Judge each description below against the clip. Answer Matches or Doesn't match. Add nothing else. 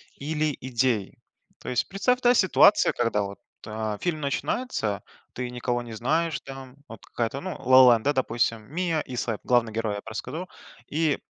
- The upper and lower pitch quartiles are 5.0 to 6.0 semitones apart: Matches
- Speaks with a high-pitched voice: Doesn't match